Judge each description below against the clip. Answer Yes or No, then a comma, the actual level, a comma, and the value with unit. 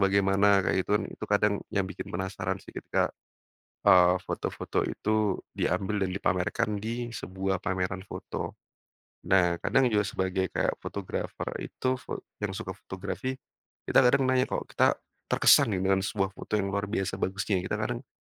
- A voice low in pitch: Yes, low, 100 Hz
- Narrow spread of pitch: Yes, narrow, 2.1 semitones